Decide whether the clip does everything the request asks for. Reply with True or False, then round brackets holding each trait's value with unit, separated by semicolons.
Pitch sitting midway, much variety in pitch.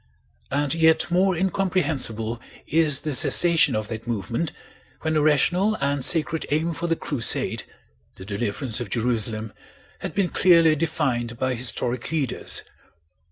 True (145 Hz; 5.7 semitones)